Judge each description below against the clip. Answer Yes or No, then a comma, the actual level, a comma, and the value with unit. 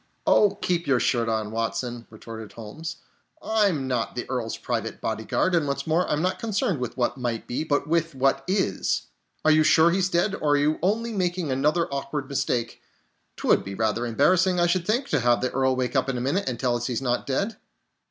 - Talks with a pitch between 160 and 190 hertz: No, medium, 140 Hz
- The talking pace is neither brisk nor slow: No, fast, 210 wpm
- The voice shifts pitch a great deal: Yes, wide, 6.1 semitones